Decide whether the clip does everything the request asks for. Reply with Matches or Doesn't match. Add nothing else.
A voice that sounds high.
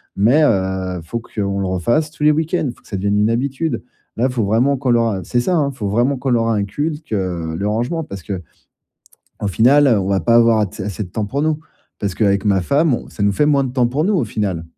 Doesn't match